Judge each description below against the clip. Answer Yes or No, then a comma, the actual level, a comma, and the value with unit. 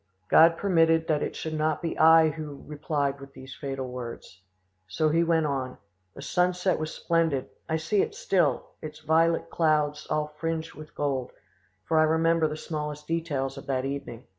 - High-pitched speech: No, medium, 155 Hz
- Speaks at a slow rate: No, average, 175 wpm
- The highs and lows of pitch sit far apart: No, narrow, 2.6 semitones